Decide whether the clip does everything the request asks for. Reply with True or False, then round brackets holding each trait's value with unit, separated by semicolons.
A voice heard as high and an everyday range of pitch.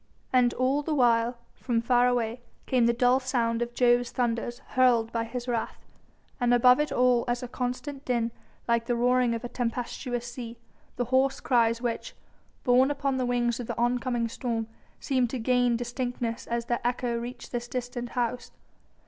False (245 Hz; 1.1 semitones)